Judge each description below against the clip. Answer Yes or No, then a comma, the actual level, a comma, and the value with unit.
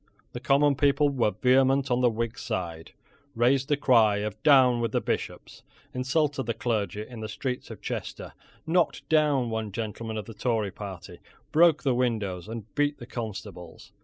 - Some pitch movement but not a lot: Yes, average, 4.3 semitones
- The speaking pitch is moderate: No, low, 120 Hz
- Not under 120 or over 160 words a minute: No, average, 170 wpm